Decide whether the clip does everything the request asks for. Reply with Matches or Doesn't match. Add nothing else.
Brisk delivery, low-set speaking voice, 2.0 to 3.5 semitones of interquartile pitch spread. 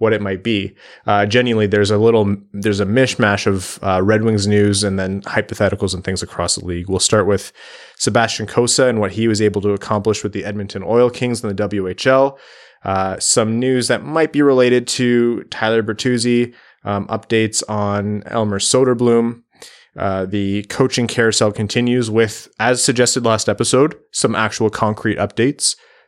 Doesn't match